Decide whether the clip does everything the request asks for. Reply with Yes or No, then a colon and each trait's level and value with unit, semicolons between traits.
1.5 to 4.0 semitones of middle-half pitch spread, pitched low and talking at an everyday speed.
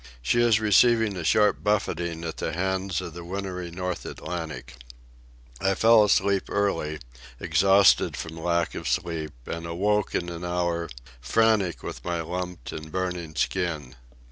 Yes: average, 2.8 semitones; very low, 90 Hz; average, 145 wpm